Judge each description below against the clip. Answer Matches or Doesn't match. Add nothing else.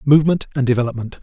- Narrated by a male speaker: Matches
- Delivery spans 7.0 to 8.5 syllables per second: Matches